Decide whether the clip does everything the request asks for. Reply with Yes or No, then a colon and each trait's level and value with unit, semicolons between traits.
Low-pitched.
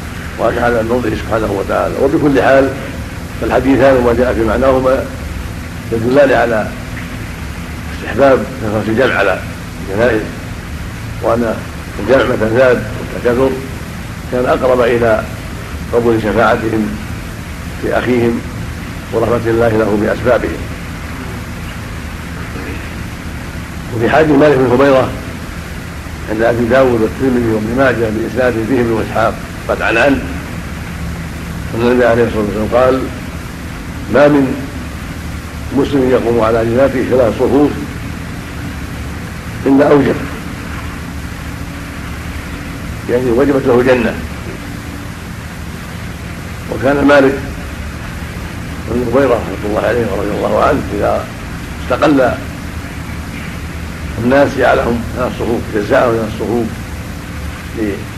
Yes: low, 105 Hz